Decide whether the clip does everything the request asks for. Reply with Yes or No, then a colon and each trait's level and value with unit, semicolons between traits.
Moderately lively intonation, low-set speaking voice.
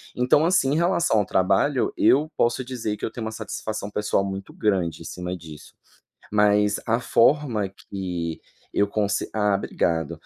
Yes: average, 4.0 semitones; low, 105 Hz